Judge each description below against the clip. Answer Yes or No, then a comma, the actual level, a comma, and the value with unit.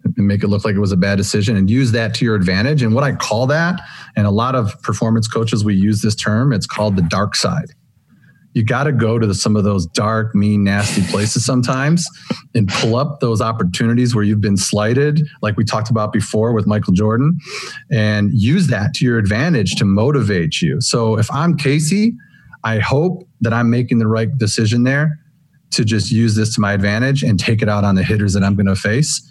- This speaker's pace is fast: Yes, fast, 220 wpm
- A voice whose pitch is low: Yes, low, 115 Hz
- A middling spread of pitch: Yes, average, 4.6 semitones